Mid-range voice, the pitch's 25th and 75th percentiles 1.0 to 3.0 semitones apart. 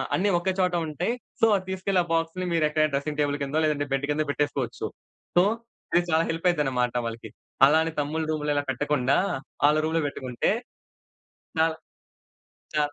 Yes: medium, 150 Hz; narrow, 2.5 semitones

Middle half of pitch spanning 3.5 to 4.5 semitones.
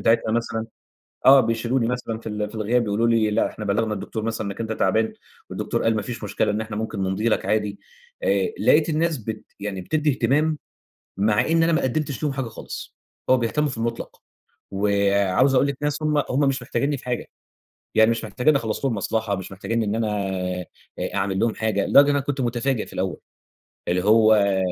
Yes: average, 4.1 semitones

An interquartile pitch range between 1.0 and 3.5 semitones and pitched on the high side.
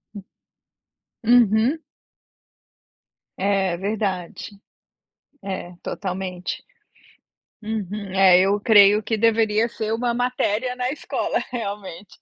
Yes: average, 2.9 semitones; high, 210 Hz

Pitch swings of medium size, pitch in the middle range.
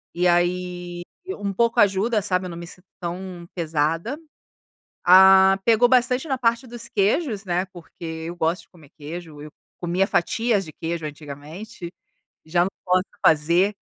Yes: average, 3.3 semitones; medium, 180 Hz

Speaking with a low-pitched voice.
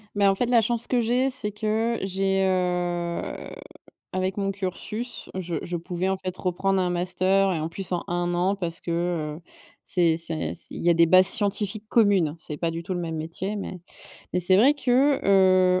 No: medium, 185 Hz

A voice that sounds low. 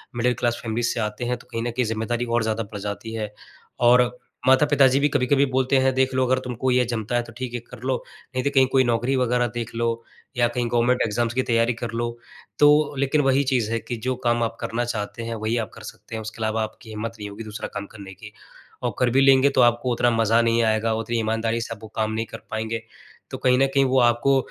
Yes: low, 120 Hz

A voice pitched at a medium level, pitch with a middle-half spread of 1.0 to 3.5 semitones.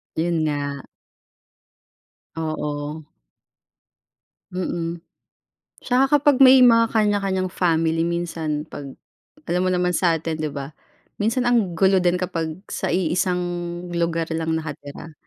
Yes: medium, 170 Hz; average, 2.9 semitones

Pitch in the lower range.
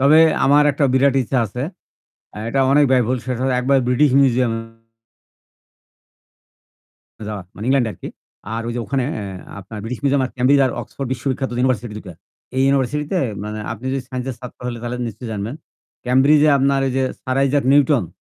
Yes: low, 130 Hz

